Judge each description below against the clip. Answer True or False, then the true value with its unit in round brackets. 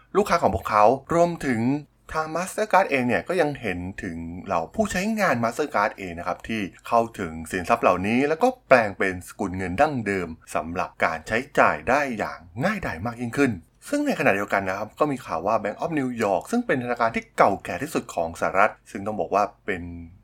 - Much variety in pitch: True (7.7 semitones)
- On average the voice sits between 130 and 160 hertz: False (120 Hz)